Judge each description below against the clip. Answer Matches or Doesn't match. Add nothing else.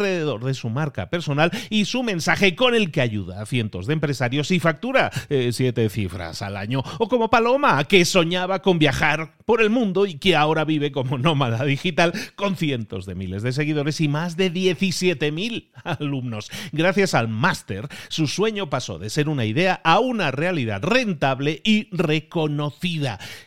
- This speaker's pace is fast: Doesn't match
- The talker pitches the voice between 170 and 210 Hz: Doesn't match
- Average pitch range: Doesn't match